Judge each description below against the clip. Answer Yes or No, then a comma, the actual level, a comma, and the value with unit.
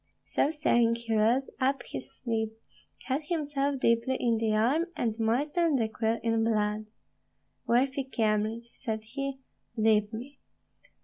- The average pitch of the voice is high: Yes, high, 230 Hz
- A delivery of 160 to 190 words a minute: No, slow, 135 wpm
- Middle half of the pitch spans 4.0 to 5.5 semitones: No, average, 3.5 semitones